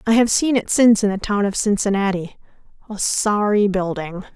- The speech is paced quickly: No, average, 165 wpm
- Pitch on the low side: No, high, 205 Hz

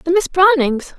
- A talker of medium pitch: No, very high, 335 Hz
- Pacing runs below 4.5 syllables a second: Yes, 4.3 syllables/s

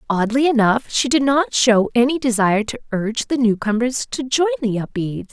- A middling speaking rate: Yes, average, 180 wpm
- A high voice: Yes, high, 240 Hz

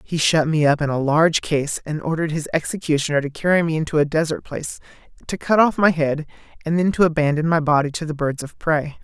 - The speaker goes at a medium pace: No, fast, 230 wpm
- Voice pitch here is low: No, medium, 155 Hz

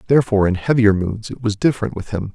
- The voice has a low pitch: Yes, low, 105 Hz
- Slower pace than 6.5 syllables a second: No, 6.9 syllables/s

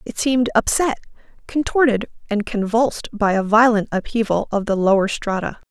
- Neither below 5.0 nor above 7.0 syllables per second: Yes, 5.4 syllables/s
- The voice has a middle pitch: No, high, 220 Hz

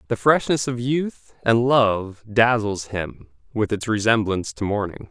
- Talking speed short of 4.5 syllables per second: Yes, 4.2 syllables/s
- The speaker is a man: Yes, male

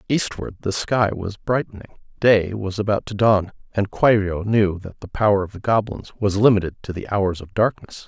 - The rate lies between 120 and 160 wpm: No, average, 195 wpm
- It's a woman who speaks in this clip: No, male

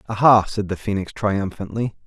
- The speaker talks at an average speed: Yes, average, 145 wpm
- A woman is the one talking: No, male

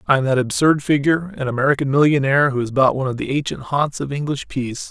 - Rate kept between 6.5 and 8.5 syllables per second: Yes, 6.8 syllables/s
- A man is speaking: Yes, male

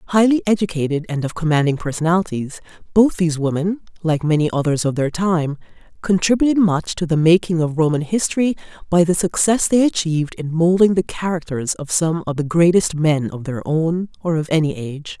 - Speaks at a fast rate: No, average, 180 wpm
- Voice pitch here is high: No, medium, 165 Hz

